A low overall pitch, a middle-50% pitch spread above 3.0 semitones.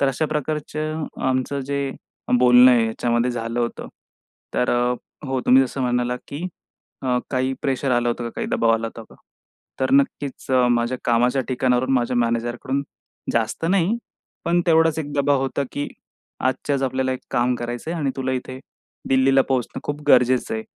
No: low, 130 Hz; narrow, 2.5 semitones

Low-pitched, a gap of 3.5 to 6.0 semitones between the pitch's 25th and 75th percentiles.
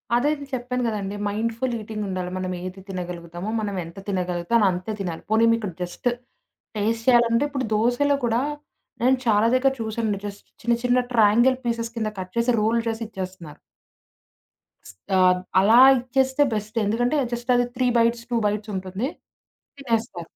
No: high, 220 Hz; average, 3.8 semitones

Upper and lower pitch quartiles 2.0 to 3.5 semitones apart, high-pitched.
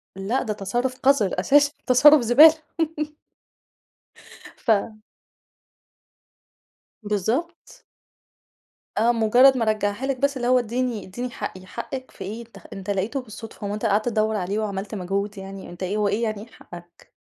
No: average, 3.9 semitones; high, 220 Hz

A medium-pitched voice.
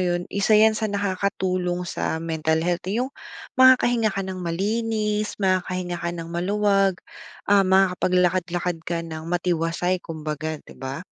Yes: medium, 180 Hz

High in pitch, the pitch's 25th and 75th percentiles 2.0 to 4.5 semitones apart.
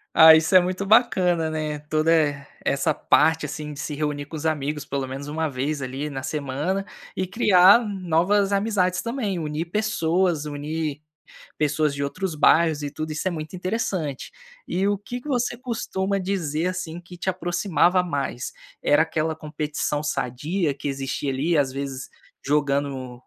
No: medium, 160 Hz; average, 4.2 semitones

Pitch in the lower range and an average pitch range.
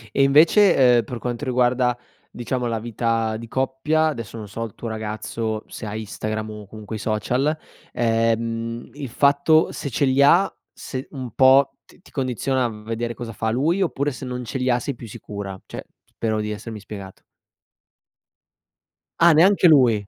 Yes: low, 120 Hz; average, 3.6 semitones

